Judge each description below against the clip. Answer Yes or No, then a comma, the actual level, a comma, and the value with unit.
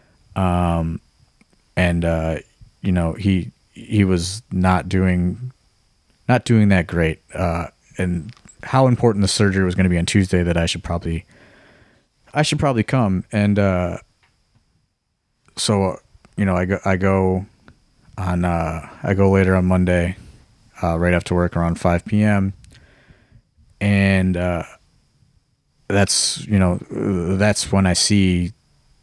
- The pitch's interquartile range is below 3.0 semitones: Yes, narrow, 2.6 semitones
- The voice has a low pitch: Yes, very low, 95 Hz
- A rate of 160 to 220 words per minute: No, average, 140 wpm